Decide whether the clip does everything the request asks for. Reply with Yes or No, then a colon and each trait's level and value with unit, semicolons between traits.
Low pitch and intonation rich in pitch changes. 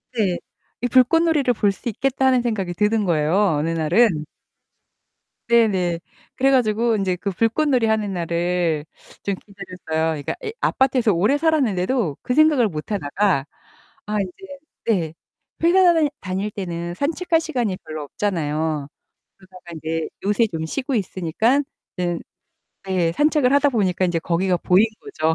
No: high, 200 Hz; wide, 6.6 semitones